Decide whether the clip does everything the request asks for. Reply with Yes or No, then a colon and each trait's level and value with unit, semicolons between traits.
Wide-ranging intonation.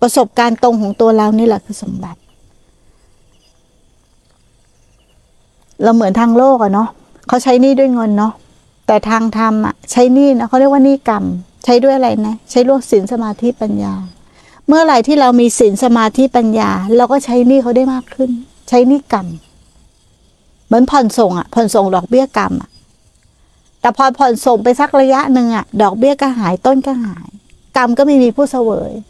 No: average, 3.4 semitones